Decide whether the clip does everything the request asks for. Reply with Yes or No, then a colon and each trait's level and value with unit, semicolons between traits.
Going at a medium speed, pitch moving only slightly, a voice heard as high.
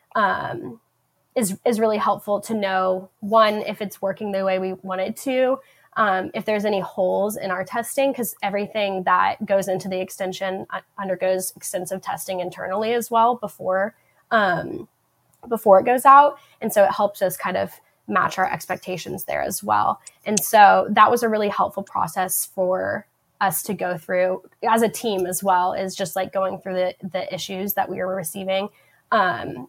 Yes: average, 180 wpm; narrow, 2.3 semitones; high, 195 Hz